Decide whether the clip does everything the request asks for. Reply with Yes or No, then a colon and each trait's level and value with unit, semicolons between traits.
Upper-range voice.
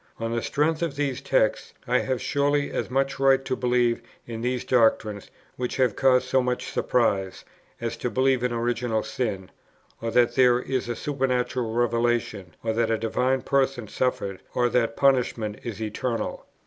No: low, 125 Hz